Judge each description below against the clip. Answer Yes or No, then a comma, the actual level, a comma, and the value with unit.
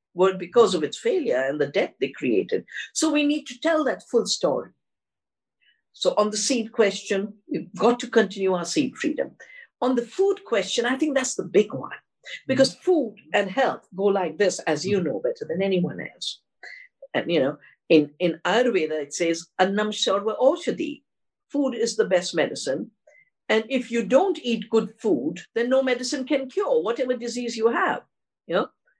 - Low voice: No, high, 235 Hz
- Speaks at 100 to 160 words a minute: No, average, 180 wpm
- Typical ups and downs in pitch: No, wide, 6.0 semitones